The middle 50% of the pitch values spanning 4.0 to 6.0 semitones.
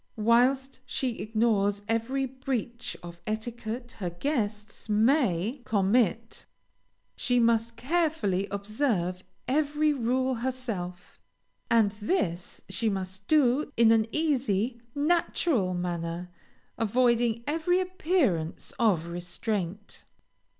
Yes: average, 4.8 semitones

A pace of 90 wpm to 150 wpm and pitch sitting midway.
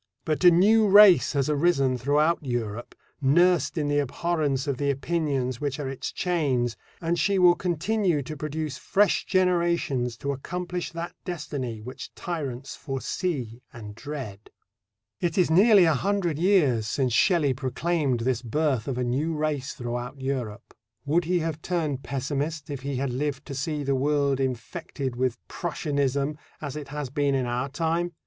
No: average, 160 wpm; medium, 145 Hz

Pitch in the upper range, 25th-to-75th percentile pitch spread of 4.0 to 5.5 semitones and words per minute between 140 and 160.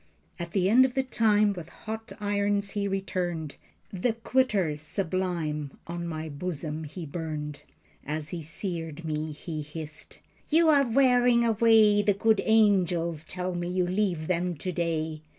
No: medium, 180 Hz; average, 4.8 semitones; average, 150 wpm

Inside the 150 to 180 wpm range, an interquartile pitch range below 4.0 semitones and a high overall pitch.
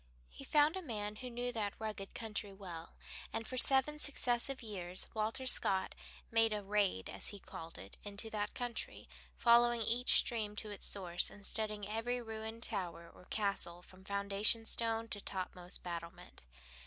Yes: average, 165 wpm; average, 3.1 semitones; high, 215 Hz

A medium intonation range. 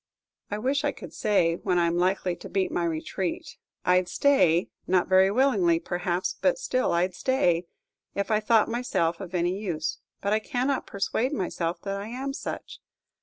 No: wide, 6.0 semitones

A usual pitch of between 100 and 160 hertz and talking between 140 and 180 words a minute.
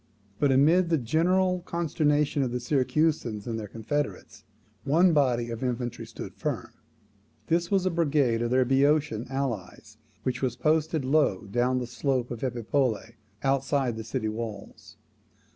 Yes: low, 135 Hz; average, 145 wpm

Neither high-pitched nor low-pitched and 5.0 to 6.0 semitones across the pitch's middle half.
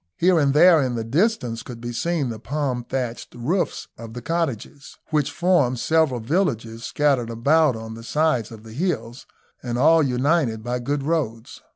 No: low, 130 Hz; wide, 5.4 semitones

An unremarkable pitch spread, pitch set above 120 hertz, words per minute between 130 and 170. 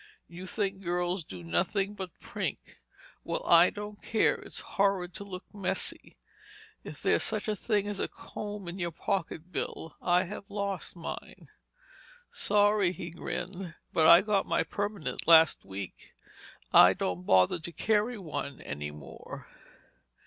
Yes: average, 3.7 semitones; medium, 185 Hz; average, 145 wpm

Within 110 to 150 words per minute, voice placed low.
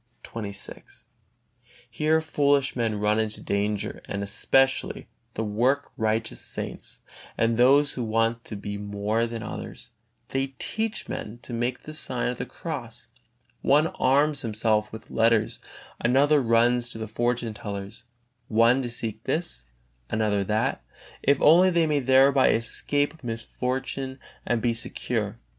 Yes: slow, 135 wpm; low, 120 Hz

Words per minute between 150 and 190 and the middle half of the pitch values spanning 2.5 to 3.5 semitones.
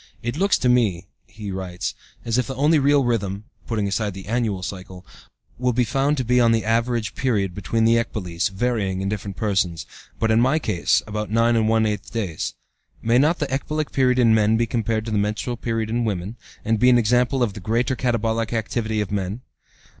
No: fast, 205 wpm; average, 3.1 semitones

